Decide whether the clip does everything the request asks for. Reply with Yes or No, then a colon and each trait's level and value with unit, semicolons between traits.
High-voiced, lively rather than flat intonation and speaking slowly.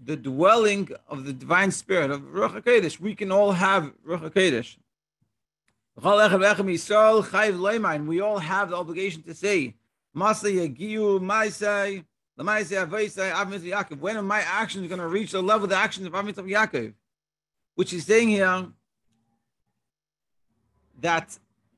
No: high, 195 Hz; average, 4.3 semitones; slow, 115 wpm